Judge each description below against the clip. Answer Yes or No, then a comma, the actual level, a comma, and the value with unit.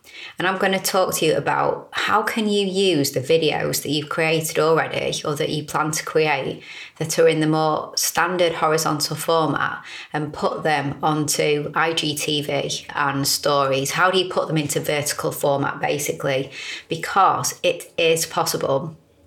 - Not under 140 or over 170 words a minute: Yes, average, 160 wpm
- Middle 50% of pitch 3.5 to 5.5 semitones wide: Yes, average, 3.9 semitones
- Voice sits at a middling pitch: Yes, medium, 160 Hz